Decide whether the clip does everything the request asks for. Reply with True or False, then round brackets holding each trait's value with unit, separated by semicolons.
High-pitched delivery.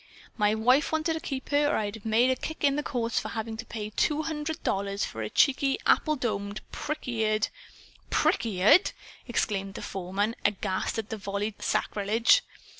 True (225 Hz)